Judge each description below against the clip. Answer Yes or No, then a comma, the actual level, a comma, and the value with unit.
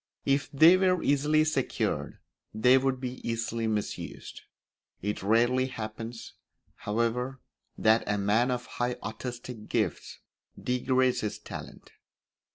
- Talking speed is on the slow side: Yes, slow, 115 wpm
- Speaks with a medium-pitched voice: No, low, 125 Hz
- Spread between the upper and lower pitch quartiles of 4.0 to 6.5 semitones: No, average, 2.8 semitones